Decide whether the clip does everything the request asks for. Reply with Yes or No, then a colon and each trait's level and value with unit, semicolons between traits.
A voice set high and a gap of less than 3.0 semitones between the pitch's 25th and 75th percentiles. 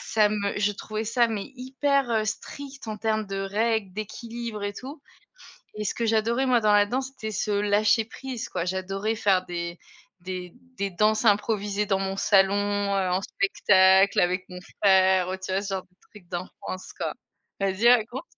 Yes: high, 205 Hz; narrow, 2.6 semitones